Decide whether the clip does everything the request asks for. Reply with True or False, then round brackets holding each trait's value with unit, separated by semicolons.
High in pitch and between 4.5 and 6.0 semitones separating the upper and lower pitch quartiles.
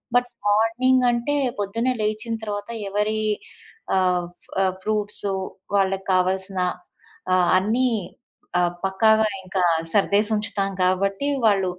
False (205 Hz; 2.4 semitones)